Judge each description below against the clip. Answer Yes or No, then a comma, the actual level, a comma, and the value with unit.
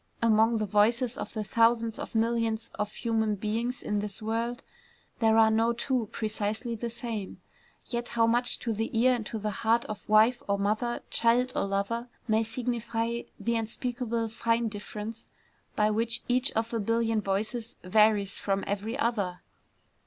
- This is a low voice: No, high, 225 Hz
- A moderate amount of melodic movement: No, narrow, 1.7 semitones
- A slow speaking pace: No, average, 165 wpm